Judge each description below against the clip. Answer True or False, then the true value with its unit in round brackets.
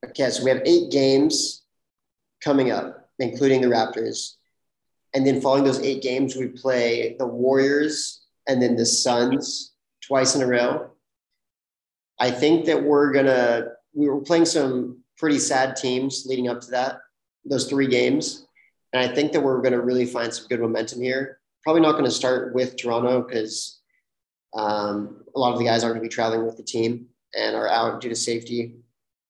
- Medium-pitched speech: False (125 Hz)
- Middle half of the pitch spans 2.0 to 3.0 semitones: True (2.4 semitones)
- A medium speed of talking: True (185 wpm)